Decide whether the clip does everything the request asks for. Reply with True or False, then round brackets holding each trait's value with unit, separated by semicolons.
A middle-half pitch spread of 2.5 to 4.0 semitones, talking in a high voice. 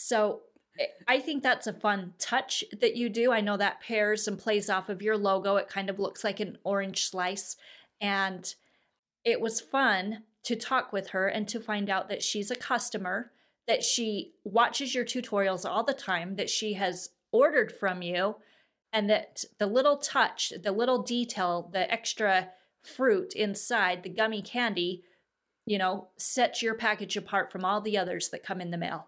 True (3.6 semitones; 210 Hz)